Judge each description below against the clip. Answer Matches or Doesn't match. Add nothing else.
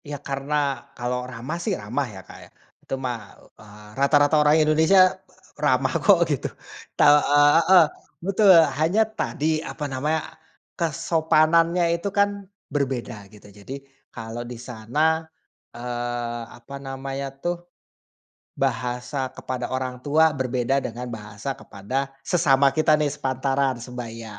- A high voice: Doesn't match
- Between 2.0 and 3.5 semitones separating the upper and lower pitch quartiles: Doesn't match